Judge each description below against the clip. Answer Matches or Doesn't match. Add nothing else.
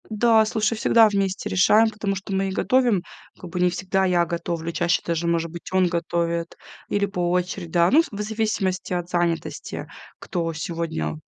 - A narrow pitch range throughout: Doesn't match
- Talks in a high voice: Doesn't match